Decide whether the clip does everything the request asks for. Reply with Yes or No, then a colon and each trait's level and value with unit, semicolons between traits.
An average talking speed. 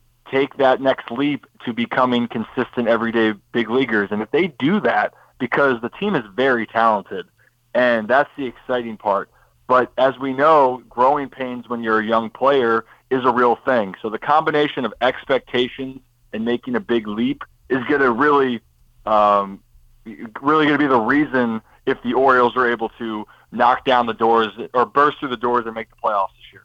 Yes: average, 180 wpm